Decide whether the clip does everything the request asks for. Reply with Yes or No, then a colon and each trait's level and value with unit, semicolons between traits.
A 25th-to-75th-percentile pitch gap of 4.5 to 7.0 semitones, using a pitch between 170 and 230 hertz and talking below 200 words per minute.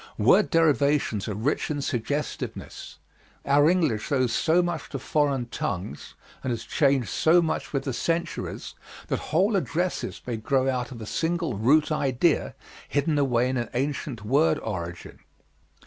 No: average, 4.8 semitones; medium, 140 Hz; average, 150 wpm